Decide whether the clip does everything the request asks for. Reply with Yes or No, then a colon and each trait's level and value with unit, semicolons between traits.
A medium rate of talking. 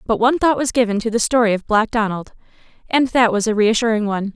No: fast, 235 wpm